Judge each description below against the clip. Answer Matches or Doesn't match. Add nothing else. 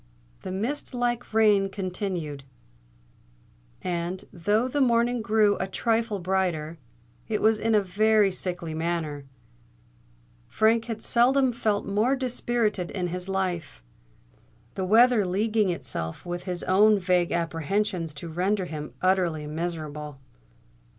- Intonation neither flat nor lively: Matches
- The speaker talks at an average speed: Doesn't match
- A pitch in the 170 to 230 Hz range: Matches